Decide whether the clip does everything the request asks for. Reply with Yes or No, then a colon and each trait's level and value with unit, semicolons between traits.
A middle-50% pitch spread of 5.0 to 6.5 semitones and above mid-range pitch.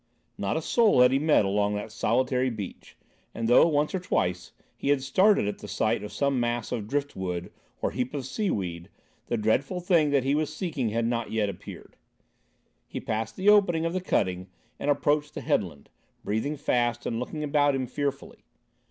No: wide, 5.5 semitones; low, 130 Hz